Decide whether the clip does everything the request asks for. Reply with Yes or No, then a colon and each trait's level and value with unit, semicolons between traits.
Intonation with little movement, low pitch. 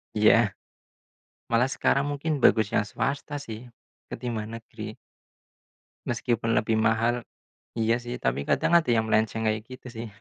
Yes: narrow, 2.2 semitones; low, 115 Hz